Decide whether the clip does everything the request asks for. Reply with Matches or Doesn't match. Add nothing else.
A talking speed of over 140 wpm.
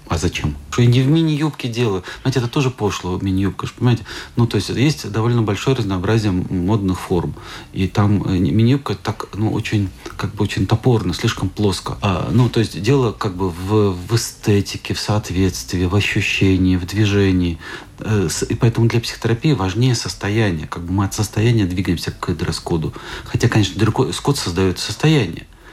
Matches